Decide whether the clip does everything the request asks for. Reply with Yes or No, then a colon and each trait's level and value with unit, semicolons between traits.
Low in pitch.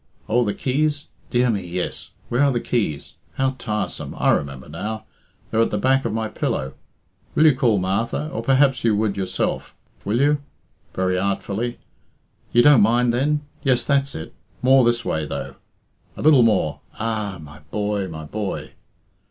Yes: low, 115 Hz